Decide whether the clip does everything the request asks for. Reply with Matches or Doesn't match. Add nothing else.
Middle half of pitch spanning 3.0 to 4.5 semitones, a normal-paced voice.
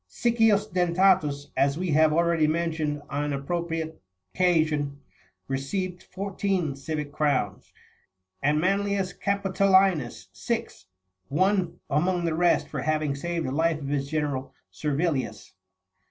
Doesn't match